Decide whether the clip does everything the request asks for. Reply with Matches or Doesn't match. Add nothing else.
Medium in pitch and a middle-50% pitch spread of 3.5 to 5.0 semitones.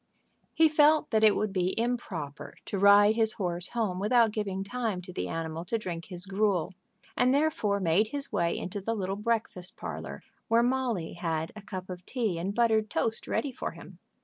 Doesn't match